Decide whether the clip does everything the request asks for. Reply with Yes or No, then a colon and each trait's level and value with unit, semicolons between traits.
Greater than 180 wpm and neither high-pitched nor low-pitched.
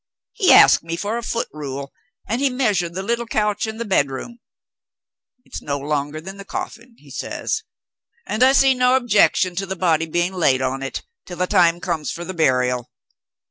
Yes: average, 190 wpm; medium, 180 Hz